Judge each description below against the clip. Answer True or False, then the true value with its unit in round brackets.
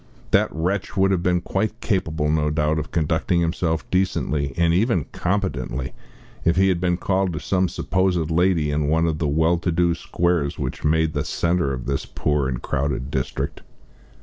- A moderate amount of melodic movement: True (3.2 semitones)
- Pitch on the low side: True (85 Hz)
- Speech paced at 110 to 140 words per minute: False (180 wpm)